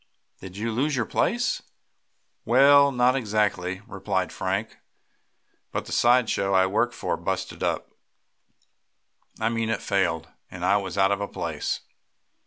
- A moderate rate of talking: Yes, average, 150 wpm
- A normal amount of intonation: Yes, average, 3.9 semitones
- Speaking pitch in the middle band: No, low, 105 Hz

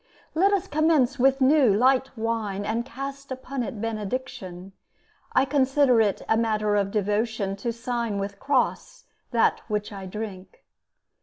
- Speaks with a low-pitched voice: No, high, 230 Hz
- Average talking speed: Yes, average, 145 wpm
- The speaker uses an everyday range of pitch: Yes, average, 4.4 semitones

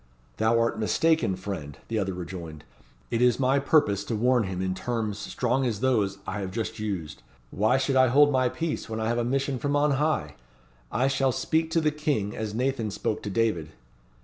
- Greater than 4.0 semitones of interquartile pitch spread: Yes, average, 5.0 semitones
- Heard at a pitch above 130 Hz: No, low, 115 Hz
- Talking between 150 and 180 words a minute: No, average, 200 wpm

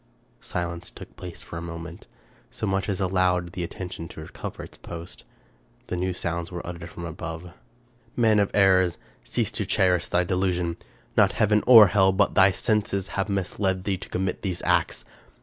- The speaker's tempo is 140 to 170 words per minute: No, average, 185 wpm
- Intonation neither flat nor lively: No, narrow, 2.1 semitones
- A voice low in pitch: Yes, very low, 90 Hz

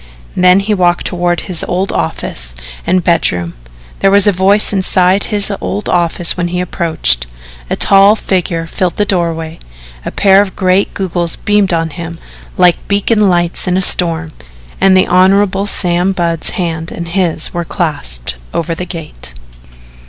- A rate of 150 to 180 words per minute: Yes, average, 160 wpm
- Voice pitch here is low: No, medium, 180 Hz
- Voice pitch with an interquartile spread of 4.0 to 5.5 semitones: No, narrow, 2.6 semitones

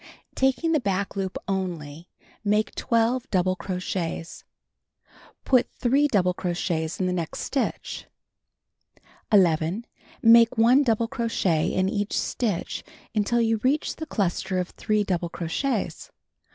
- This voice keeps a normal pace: No, slow, 125 wpm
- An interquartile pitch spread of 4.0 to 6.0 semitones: Yes, average, 4.5 semitones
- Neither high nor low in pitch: No, high, 200 Hz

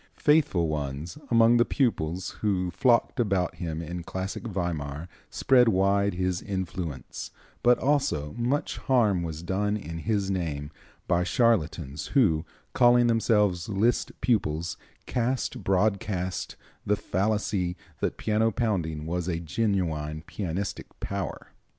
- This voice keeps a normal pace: No, slow, 120 wpm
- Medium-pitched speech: No, very low, 95 Hz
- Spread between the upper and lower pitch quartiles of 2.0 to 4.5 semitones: No, average, 5.1 semitones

